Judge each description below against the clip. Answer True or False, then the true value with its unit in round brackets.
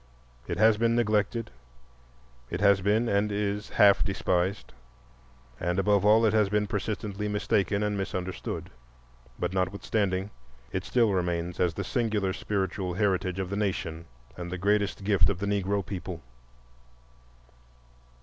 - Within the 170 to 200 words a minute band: False (140 wpm)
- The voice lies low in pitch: True (100 Hz)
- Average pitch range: False (2.1 semitones)